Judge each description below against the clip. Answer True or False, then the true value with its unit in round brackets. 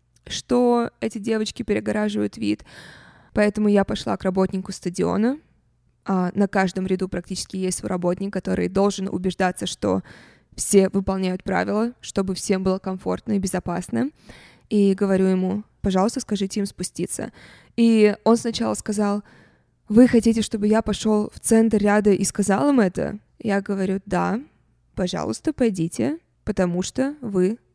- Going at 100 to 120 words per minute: False (135 wpm)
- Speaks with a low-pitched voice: False (200 Hz)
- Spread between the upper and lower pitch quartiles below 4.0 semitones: True (2.6 semitones)